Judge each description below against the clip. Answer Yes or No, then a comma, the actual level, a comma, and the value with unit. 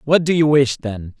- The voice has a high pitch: No, low, 135 Hz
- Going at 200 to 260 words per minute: Yes, fast, 250 wpm